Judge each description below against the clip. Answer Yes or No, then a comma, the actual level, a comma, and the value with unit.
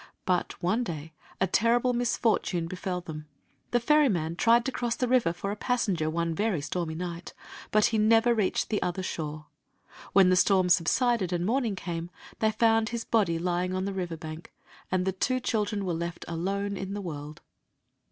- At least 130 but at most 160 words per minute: No, average, 180 wpm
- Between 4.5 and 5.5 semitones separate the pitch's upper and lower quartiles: Yes, average, 4.8 semitones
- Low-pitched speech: No, medium, 185 Hz